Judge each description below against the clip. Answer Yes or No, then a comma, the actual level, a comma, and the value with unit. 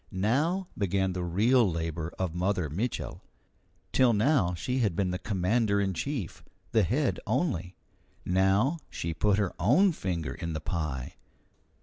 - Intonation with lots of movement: Yes, wide, 5.8 semitones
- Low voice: Yes, very low, 95 Hz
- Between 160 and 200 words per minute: No, average, 145 wpm